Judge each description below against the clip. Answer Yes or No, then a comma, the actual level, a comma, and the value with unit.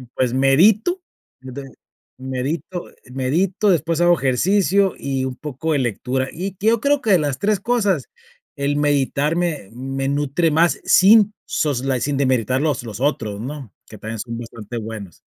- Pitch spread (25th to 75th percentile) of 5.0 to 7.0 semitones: Yes, wide, 5.5 semitones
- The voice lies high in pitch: No, medium, 145 Hz